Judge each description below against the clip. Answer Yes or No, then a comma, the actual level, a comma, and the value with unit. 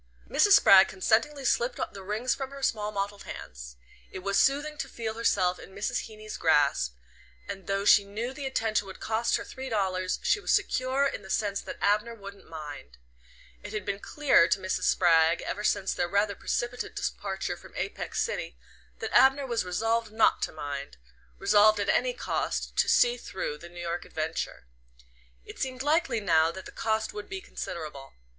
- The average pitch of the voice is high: Yes, high, 205 Hz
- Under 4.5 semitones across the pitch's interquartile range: No, average, 4.8 semitones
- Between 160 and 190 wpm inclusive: Yes, average, 180 wpm